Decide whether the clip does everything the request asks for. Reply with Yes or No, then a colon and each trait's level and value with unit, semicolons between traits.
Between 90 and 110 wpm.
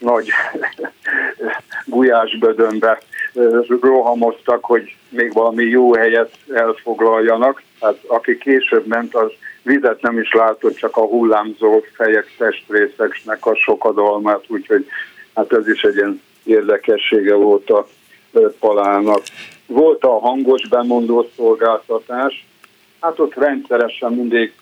Yes: slow, 105 wpm